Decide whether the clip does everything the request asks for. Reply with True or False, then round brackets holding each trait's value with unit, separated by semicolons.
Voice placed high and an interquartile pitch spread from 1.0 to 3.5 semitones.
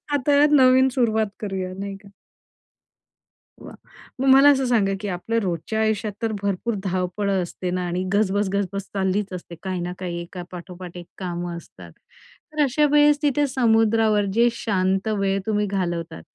False (200 Hz; 3.9 semitones)